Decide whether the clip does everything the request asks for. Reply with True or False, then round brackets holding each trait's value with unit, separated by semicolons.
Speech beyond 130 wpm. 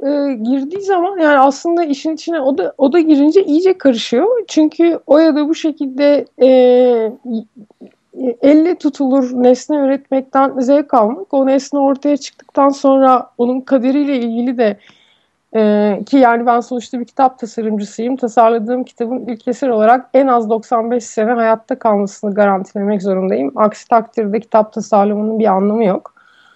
True (140 wpm)